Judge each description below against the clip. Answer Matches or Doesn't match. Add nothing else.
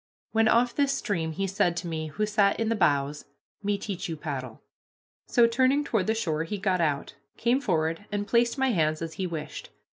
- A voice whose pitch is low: Doesn't match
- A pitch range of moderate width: Doesn't match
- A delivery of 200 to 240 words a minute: Matches